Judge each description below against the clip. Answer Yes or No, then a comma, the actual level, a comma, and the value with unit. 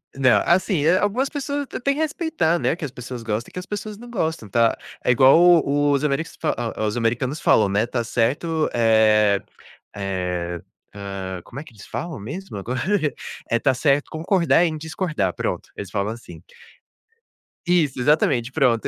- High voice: No, low, 135 Hz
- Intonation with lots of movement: Yes, wide, 7.1 semitones